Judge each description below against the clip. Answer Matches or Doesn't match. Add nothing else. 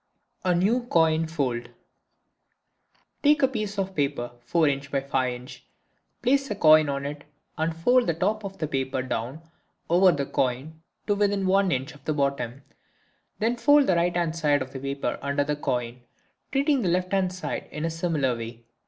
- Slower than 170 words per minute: Doesn't match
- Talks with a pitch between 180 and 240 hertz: Doesn't match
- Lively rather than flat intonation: Matches